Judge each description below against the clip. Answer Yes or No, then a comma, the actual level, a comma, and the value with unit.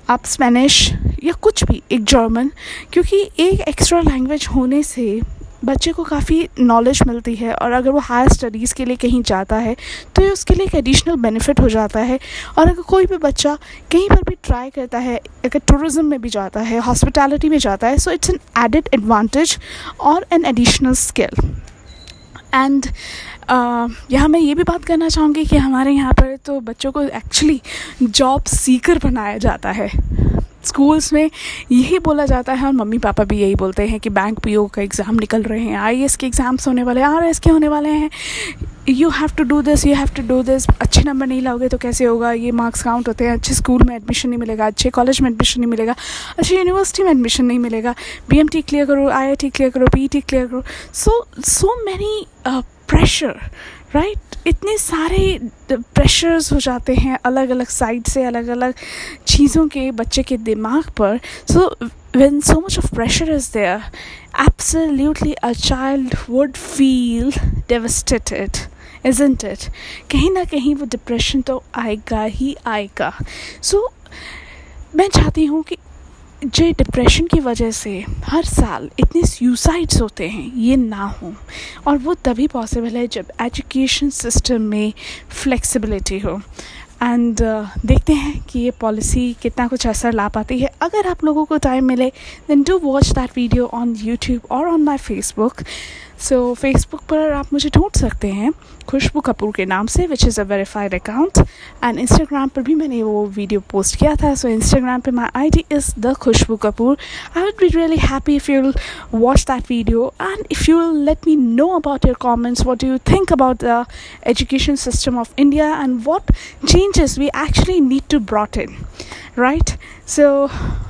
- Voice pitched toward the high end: Yes, very high, 265 Hz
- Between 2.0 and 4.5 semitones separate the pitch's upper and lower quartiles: Yes, average, 4.1 semitones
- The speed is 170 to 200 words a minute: Yes, average, 175 wpm